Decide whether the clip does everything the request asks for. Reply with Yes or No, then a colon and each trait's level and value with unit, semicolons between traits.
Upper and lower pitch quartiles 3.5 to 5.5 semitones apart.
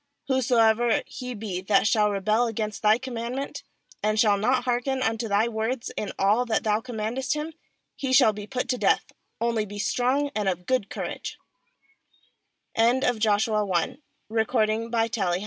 No: average, 3.0 semitones